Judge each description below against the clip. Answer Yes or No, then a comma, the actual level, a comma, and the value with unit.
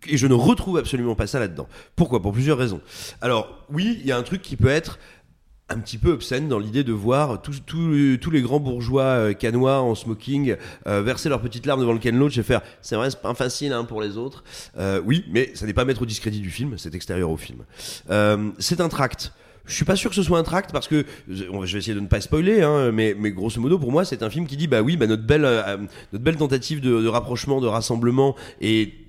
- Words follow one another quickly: Yes, fast, 255 wpm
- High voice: No, low, 125 Hz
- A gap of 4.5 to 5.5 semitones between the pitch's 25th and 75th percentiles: Yes, average, 4.9 semitones